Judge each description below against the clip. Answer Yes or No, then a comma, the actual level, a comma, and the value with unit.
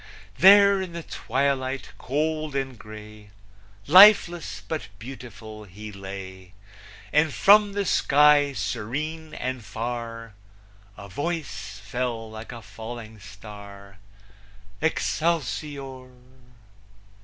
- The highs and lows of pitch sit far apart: Yes, wide, 6.3 semitones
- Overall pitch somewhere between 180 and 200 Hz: No, low, 130 Hz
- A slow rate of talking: Yes, slow, 95 wpm